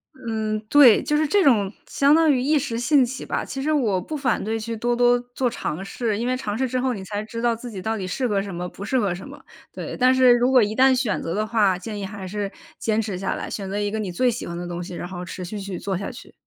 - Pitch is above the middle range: Yes, high, 220 Hz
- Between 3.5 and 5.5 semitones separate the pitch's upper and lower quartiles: Yes, average, 4.4 semitones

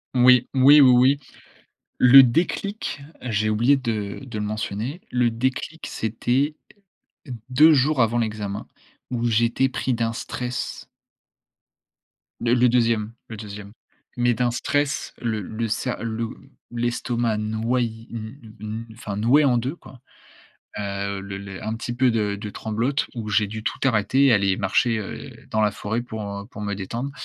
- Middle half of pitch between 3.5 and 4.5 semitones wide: No, average, 2.9 semitones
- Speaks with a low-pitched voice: Yes, low, 115 Hz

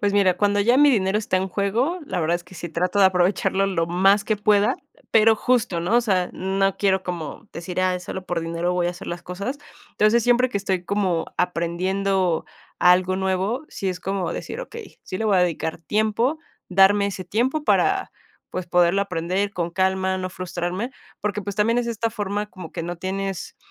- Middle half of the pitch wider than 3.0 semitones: No, narrow, 2.6 semitones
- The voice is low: No, high, 190 Hz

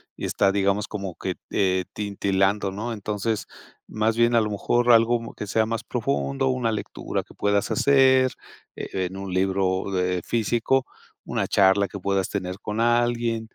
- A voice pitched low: Yes, low, 105 Hz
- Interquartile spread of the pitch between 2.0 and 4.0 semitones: Yes, average, 3.1 semitones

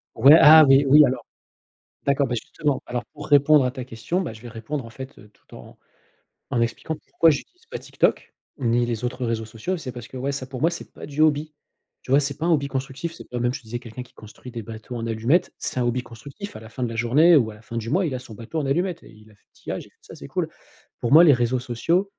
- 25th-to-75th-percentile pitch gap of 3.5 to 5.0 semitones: Yes, average, 4.3 semitones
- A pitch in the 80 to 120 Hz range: No, low, 130 Hz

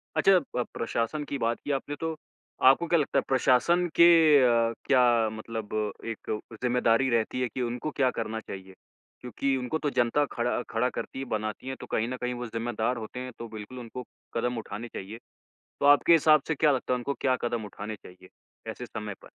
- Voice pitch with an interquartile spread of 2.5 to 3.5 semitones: Yes, average, 2.9 semitones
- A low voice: Yes, low, 125 Hz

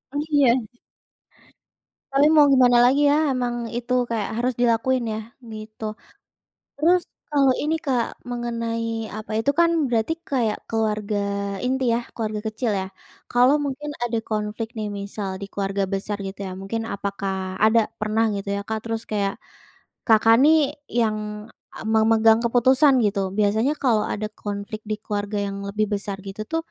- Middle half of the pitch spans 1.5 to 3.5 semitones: Yes, average, 3.2 semitones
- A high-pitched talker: Yes, high, 225 Hz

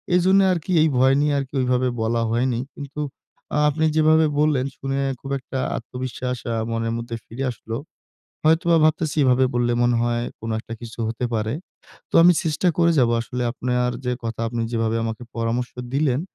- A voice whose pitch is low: Yes, low, 125 Hz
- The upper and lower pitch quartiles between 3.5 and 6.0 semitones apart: Yes, average, 4.1 semitones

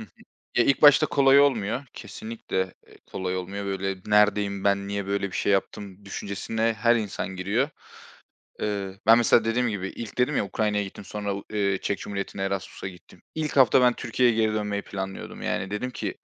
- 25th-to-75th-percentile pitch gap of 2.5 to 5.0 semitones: Yes, average, 2.8 semitones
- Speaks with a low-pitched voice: Yes, low, 105 Hz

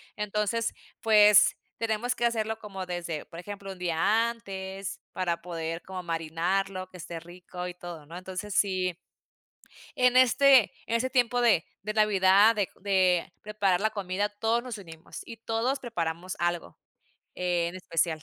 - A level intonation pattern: No, average, 3.9 semitones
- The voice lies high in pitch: Yes, high, 195 Hz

